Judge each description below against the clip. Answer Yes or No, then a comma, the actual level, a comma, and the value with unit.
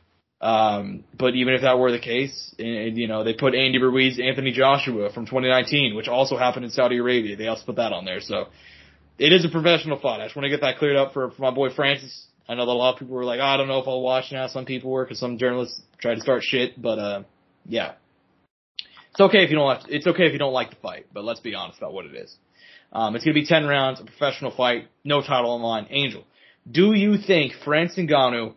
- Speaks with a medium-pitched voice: No, low, 130 Hz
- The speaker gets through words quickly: Yes, fast, 255 wpm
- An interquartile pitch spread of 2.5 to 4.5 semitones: Yes, average, 2.8 semitones